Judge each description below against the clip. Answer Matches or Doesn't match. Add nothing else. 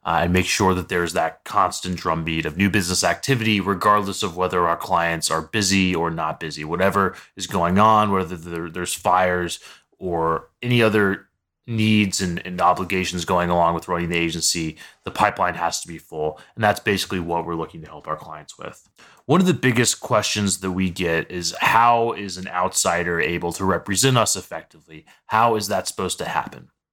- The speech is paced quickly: Doesn't match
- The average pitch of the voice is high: Doesn't match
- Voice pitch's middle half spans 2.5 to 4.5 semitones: Matches